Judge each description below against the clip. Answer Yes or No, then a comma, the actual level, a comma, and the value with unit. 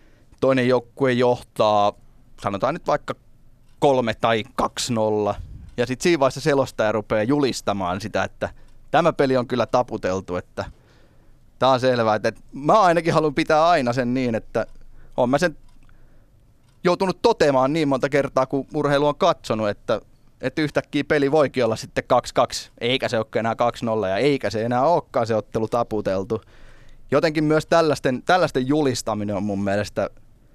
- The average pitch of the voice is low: Yes, low, 125 Hz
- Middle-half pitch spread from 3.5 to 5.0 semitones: Yes, average, 4.1 semitones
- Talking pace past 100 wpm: Yes, fast, 155 wpm